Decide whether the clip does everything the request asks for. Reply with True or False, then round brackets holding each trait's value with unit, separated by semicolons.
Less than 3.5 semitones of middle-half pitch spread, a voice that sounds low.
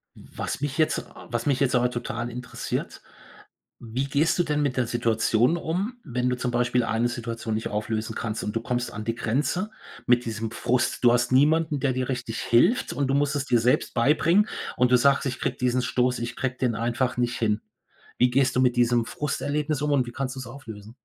True (2.9 semitones; 125 Hz)